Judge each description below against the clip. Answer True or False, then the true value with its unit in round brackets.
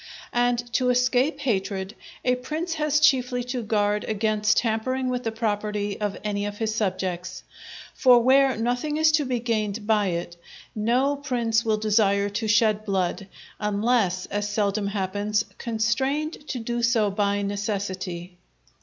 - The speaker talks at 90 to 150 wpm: True (145 wpm)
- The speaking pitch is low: False (220 Hz)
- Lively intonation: False (3.5 semitones)